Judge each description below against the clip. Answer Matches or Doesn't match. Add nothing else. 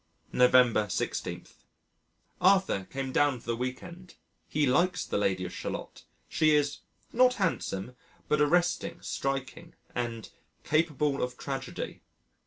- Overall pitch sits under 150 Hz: Matches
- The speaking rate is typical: Doesn't match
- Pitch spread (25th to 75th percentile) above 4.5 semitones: Matches